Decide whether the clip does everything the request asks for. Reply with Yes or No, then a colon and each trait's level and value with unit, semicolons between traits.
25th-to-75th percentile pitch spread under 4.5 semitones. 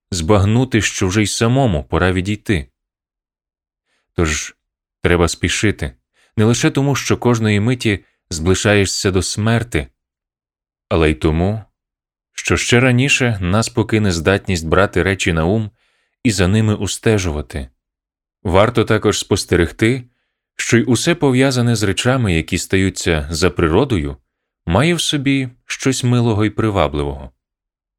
No: wide, 5.6 semitones